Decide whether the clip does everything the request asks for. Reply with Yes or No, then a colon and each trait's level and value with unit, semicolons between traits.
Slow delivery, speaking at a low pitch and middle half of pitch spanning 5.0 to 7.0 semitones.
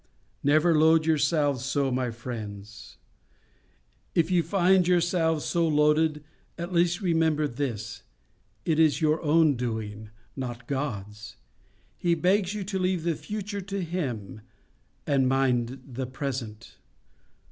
No: slow, 125 wpm; medium, 150 Hz; wide, 5.4 semitones